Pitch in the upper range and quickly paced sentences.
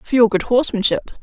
No: high, 225 Hz; average, 195 wpm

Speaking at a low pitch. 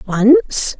No: very high, 255 Hz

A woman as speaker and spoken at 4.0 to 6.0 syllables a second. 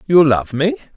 No: male; 4.6 syllables/s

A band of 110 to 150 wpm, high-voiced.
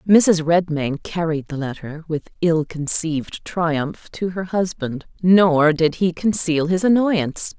No: average, 140 wpm; medium, 165 Hz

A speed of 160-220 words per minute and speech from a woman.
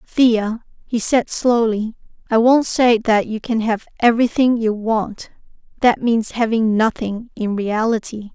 No: slow, 135 wpm; female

